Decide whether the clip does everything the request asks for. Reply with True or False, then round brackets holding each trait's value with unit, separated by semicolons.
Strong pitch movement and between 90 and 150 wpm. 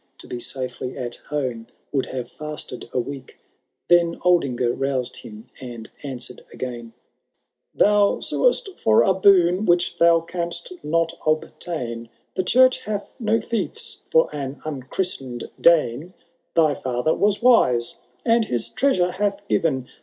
True (6.7 semitones; 140 wpm)